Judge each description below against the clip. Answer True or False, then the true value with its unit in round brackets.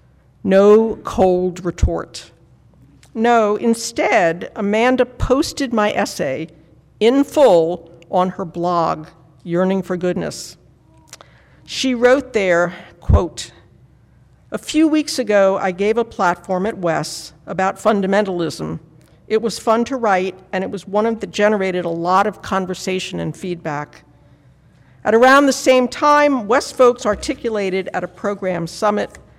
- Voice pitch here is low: False (200 Hz)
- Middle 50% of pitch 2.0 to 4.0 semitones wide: False (4.4 semitones)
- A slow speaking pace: True (125 wpm)